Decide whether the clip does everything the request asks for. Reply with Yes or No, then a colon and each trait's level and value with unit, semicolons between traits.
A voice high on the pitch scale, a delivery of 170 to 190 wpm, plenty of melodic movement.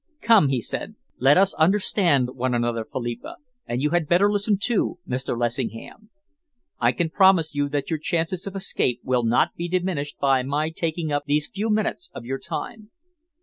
No: medium, 150 Hz; average, 180 wpm; wide, 6.6 semitones